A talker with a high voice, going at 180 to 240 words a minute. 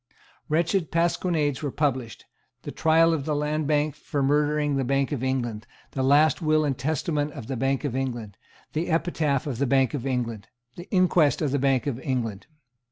No: medium, 145 Hz; average, 185 wpm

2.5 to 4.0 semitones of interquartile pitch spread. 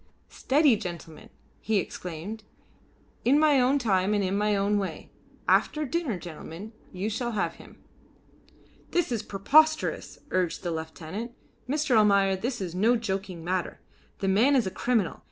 No: average, 4.9 semitones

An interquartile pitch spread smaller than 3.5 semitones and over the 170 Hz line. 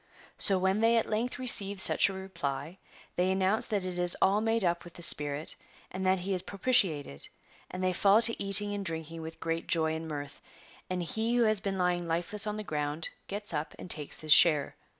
No: average, 3.8 semitones; medium, 185 Hz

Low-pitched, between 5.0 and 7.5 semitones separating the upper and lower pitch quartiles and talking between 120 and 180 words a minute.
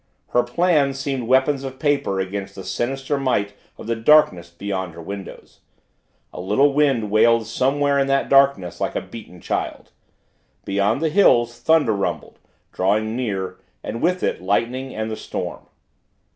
Yes: low, 120 Hz; wide, 5.4 semitones; average, 155 wpm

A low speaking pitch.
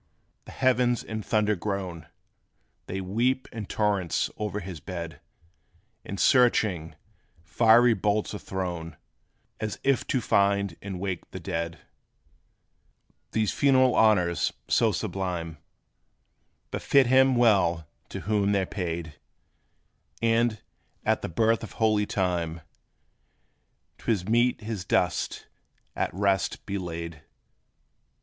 Yes: low, 100 Hz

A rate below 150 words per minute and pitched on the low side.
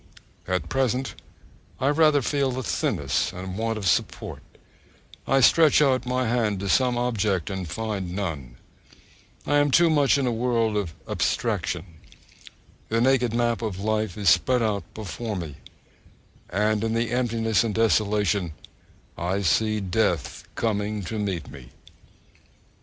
Yes: average, 140 wpm; low, 110 Hz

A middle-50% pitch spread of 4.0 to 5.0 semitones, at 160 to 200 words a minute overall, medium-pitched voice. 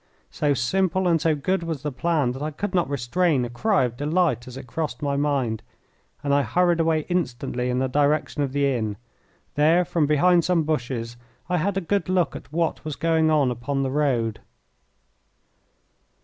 Yes: average, 4.7 semitones; average, 190 wpm; medium, 150 Hz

